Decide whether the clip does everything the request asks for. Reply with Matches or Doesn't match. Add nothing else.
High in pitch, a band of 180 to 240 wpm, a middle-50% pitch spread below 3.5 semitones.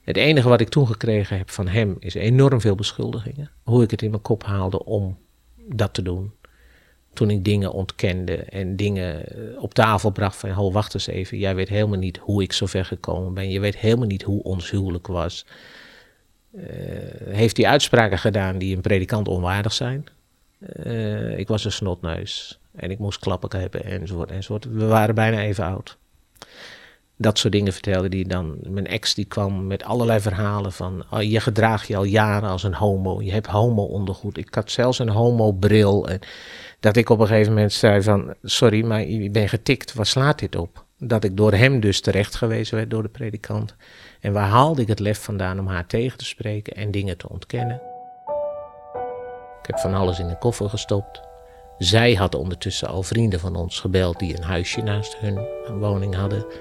Doesn't match